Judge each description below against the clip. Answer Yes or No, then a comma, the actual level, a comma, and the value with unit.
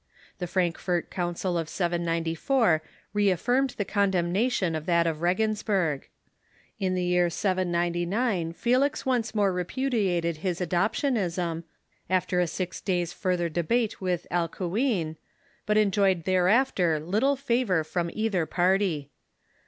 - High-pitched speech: No, medium, 180 Hz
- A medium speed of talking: No, slow, 115 wpm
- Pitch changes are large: No, average, 3.5 semitones